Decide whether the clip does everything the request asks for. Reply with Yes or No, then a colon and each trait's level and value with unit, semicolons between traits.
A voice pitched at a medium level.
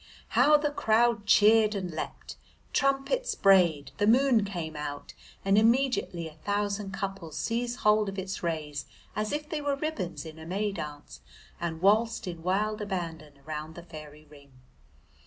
No: high, 195 Hz